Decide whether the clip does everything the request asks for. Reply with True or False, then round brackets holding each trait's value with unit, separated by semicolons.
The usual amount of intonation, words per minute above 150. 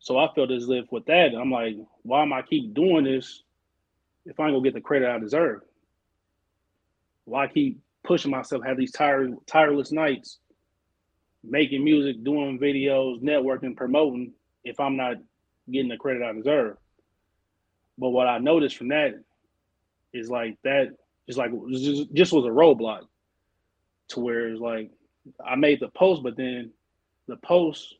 False (6.5 semitones; 160 wpm)